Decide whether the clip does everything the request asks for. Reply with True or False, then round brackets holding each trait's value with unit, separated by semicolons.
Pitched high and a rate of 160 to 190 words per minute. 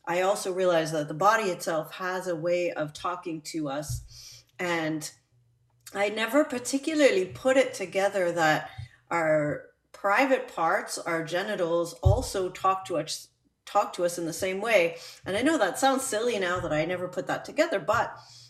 False (180 Hz; 170 wpm)